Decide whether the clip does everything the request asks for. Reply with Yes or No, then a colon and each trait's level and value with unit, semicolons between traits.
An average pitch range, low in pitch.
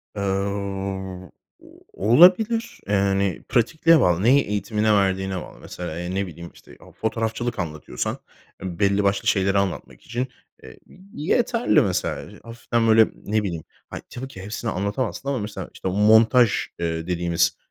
Yes: average, 3.9 semitones; low, 100 Hz